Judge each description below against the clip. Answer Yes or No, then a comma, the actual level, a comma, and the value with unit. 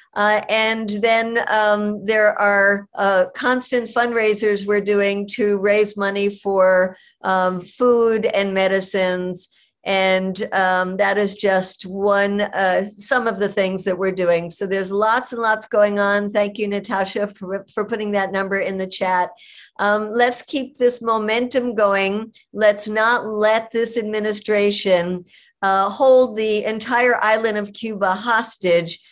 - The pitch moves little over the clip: Yes, narrow, 2.3 semitones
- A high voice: Yes, high, 205 Hz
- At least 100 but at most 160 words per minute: Yes, average, 145 wpm